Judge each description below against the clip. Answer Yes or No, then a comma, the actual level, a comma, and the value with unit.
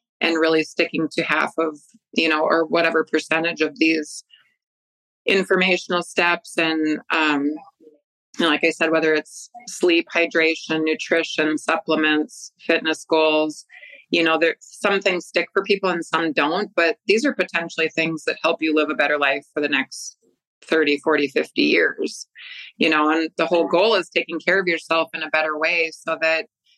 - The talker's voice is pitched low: No, medium, 160 Hz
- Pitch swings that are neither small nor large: No, narrow, 1.9 semitones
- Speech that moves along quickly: No, average, 170 wpm